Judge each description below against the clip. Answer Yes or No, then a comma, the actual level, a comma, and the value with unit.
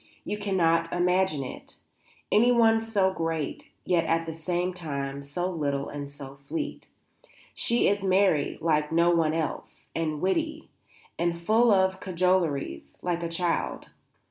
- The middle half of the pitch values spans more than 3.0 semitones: Yes, average, 3.5 semitones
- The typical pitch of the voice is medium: Yes, medium, 170 Hz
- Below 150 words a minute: Yes, average, 140 wpm